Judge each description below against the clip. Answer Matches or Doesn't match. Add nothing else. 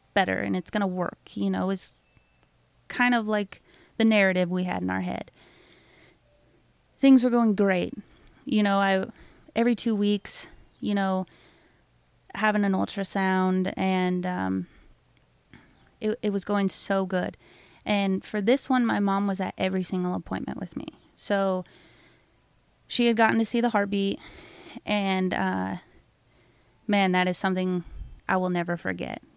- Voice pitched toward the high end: Matches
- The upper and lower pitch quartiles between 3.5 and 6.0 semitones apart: Doesn't match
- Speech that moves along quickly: Doesn't match